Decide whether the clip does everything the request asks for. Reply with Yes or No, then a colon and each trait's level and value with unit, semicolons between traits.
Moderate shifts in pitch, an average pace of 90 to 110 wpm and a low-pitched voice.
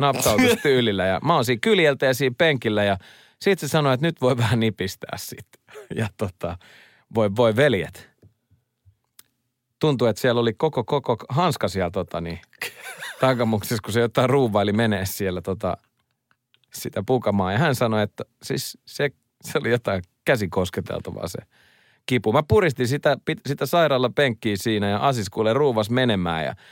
No: average, 4.9 semitones; fast, 155 wpm; low, 120 Hz